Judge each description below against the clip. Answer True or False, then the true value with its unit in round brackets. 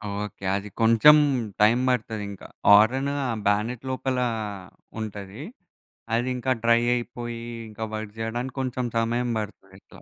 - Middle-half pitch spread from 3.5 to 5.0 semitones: False (2.8 semitones)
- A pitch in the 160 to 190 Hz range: False (115 Hz)